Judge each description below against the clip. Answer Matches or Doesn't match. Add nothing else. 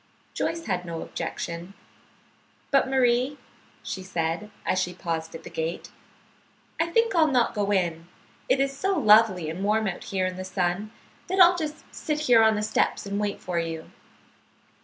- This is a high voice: Matches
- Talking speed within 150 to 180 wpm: Matches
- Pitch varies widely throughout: Matches